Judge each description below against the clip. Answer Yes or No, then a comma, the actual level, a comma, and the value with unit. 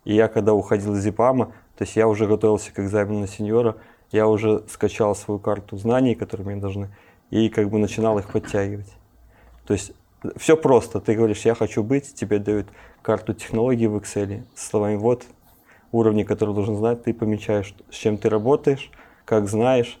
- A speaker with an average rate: No, fast, 180 wpm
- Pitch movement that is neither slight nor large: No, narrow, 1.6 semitones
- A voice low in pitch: Yes, low, 110 Hz